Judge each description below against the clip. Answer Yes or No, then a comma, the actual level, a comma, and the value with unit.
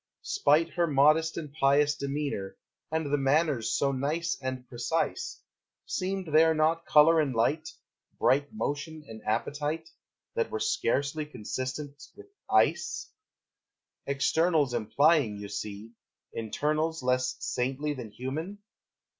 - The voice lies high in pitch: No, medium, 145 Hz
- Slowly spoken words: Yes, slow, 120 wpm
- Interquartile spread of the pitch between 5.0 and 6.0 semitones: No, average, 3.7 semitones